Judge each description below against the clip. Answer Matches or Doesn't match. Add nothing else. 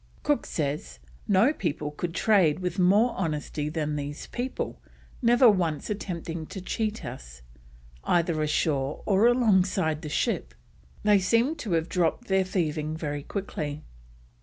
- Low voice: Doesn't match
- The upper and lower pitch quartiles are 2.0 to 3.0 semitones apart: Doesn't match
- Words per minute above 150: Doesn't match